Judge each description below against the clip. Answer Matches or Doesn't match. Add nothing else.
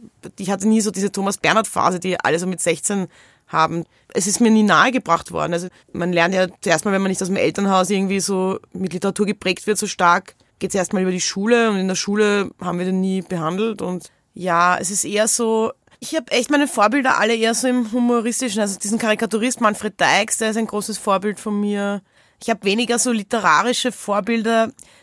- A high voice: Matches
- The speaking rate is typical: Doesn't match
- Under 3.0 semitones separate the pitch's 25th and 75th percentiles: Doesn't match